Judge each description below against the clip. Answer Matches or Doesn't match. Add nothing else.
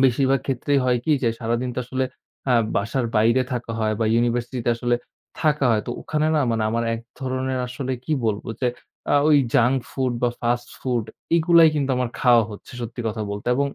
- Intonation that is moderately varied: Doesn't match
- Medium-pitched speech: Doesn't match